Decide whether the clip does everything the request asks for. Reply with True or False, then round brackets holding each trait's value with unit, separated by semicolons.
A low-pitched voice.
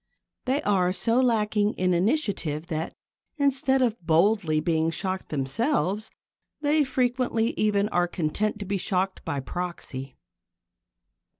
False (200 Hz)